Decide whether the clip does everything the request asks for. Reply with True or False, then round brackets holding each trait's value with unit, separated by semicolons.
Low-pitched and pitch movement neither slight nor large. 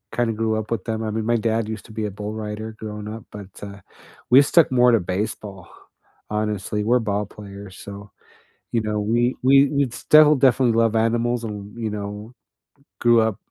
False (110 Hz; 2.1 semitones)